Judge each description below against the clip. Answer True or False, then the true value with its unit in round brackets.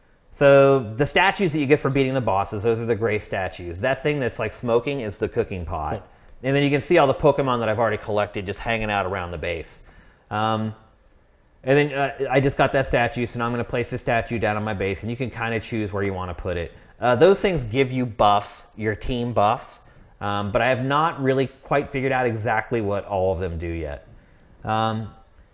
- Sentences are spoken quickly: True (235 wpm)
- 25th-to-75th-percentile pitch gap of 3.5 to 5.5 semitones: True (4.6 semitones)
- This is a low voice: True (115 Hz)